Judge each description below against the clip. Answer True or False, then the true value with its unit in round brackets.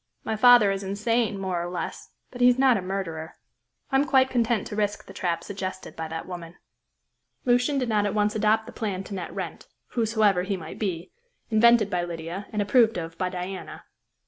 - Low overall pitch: False (205 Hz)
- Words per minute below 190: False (200 wpm)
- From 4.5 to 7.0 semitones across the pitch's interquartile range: False (4.0 semitones)